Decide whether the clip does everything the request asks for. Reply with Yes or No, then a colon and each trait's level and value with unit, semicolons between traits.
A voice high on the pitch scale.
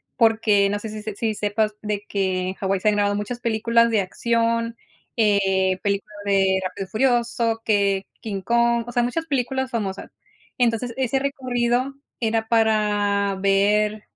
Yes: high, 215 Hz